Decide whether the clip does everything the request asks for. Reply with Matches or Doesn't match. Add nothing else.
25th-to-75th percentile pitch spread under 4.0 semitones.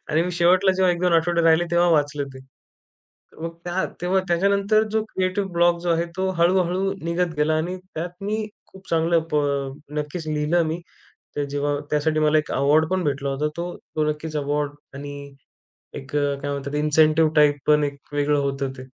Matches